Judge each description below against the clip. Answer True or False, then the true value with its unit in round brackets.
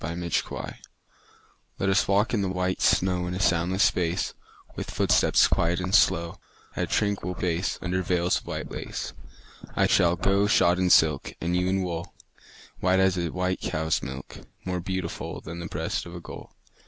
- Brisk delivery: False (180 wpm)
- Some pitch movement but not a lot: False (1.6 semitones)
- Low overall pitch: True (90 Hz)